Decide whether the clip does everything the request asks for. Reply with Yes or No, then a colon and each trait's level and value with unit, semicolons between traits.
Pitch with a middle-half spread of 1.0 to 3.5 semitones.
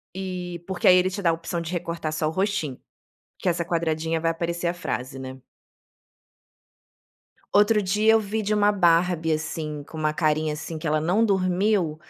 Yes: average, 3.2 semitones